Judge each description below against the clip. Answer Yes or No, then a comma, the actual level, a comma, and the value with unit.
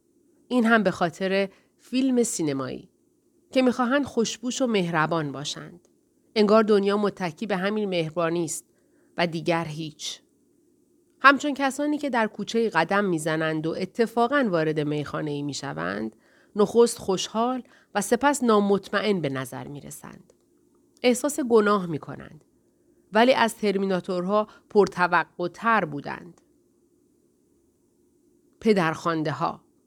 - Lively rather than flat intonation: Yes, wide, 7.5 semitones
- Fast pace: No, slow, 105 wpm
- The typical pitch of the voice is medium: No, high, 210 Hz